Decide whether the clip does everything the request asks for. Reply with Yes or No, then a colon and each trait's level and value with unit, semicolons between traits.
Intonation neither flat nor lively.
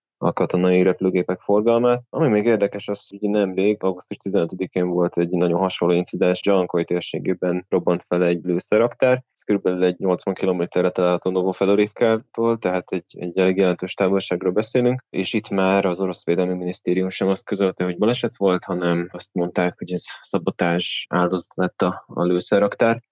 No: narrow, 2.1 semitones